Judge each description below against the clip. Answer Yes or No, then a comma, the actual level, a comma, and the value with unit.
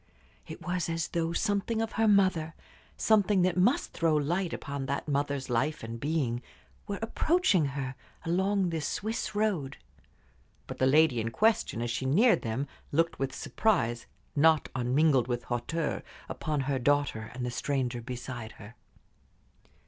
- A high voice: No, medium, 150 Hz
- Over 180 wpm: No, average, 150 wpm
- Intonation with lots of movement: Yes, wide, 6.0 semitones